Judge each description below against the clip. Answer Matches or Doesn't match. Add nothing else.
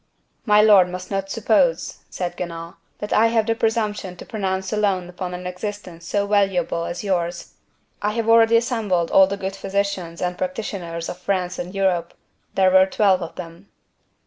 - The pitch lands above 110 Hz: Matches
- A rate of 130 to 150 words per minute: Doesn't match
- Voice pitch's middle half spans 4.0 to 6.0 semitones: Doesn't match